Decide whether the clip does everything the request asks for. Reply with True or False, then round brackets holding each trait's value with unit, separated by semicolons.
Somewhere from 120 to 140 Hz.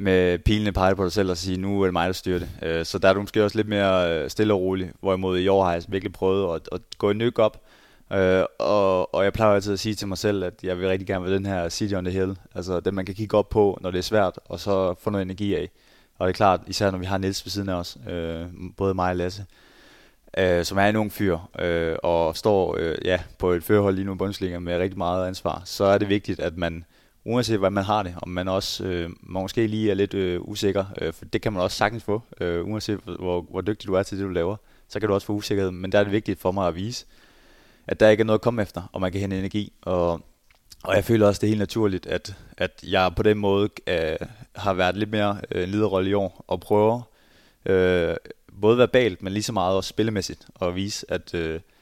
False (95 Hz)